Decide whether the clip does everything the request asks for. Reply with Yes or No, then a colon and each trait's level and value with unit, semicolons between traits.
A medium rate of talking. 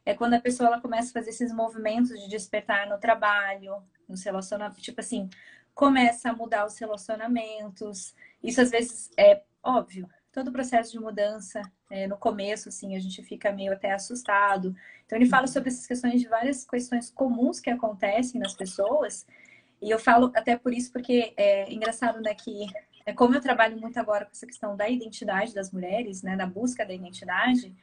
Yes: average, 185 wpm